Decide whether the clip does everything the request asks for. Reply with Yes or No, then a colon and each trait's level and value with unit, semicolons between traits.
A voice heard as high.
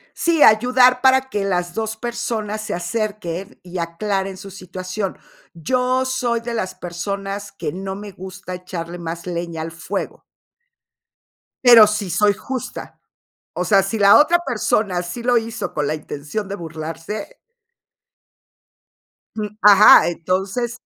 Yes: high, 200 Hz